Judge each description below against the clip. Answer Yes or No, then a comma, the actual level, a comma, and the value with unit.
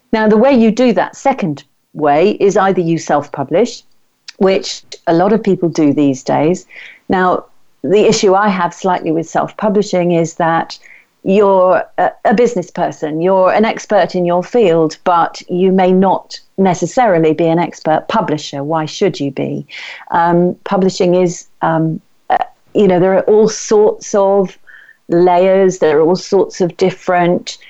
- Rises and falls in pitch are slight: No, average, 3.2 semitones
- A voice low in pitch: No, medium, 180 Hz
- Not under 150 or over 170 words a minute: Yes, average, 160 wpm